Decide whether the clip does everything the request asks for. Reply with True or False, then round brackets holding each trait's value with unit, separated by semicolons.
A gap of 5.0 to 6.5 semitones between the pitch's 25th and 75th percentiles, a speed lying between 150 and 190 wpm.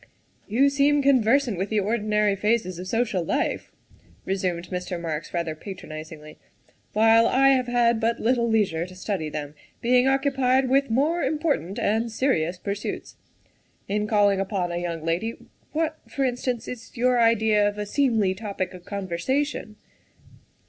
True (5.3 semitones; 155 wpm)